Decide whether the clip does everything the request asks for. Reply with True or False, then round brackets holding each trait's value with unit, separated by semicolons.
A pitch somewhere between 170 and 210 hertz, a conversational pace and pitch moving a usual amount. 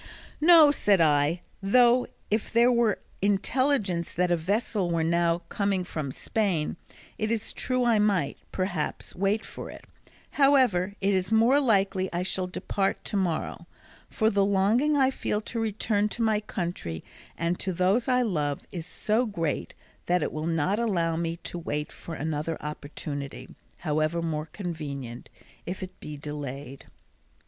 True (185 Hz; 155 wpm; 5.0 semitones)